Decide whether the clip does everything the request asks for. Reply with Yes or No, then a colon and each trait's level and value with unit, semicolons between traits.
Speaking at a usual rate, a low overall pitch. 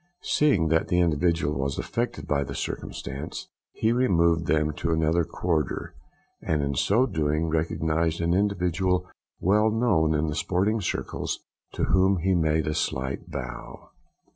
Yes: average, 145 wpm; very low, 85 Hz